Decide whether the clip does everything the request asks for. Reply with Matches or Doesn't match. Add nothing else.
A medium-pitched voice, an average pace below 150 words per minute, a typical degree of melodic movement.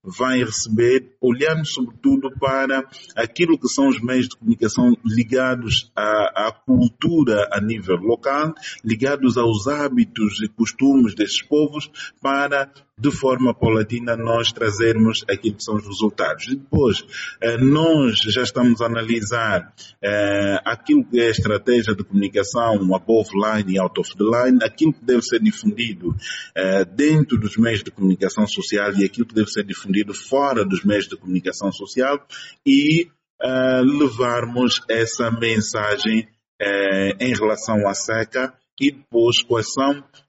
Doesn't match